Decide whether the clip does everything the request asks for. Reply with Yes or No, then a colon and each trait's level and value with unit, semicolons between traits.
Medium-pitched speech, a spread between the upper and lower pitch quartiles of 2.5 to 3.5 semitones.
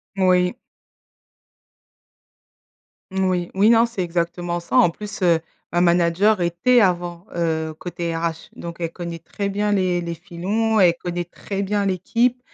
Yes: medium, 180 Hz; average, 2.8 semitones